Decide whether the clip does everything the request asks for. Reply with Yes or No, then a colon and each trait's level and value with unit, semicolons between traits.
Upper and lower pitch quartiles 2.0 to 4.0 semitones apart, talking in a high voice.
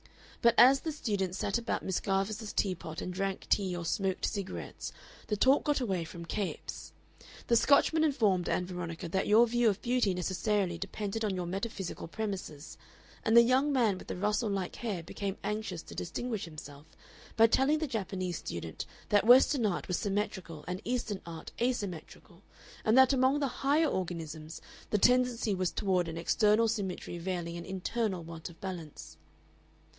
No: average, 4.7 semitones; high, 200 Hz